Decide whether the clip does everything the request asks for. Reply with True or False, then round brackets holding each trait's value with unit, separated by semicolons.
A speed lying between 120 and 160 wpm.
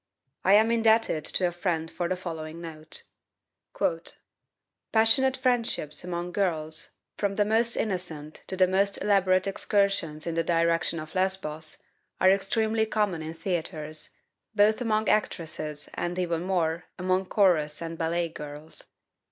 True (135 wpm)